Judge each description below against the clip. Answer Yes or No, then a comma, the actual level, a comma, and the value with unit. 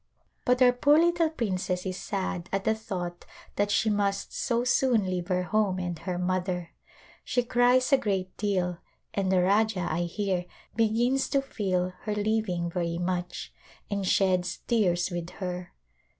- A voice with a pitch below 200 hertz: Yes, high, 190 Hz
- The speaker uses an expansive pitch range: No, average, 3.7 semitones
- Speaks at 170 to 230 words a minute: No, average, 160 wpm